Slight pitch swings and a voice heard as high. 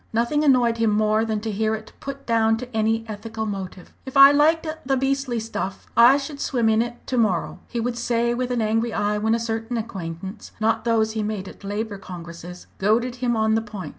Yes: narrow, 2.1 semitones; high, 225 Hz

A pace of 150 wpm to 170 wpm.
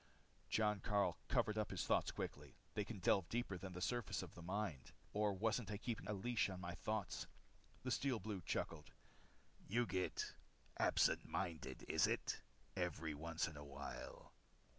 Yes: average, 165 wpm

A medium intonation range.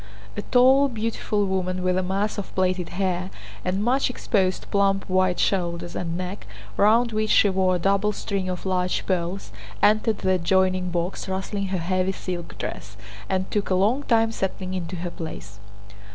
No: narrow, 2.1 semitones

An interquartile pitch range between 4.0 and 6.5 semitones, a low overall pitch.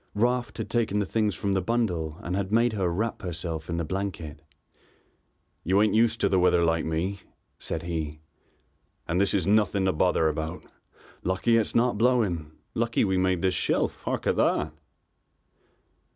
Yes: average, 4.4 semitones; very low, 95 Hz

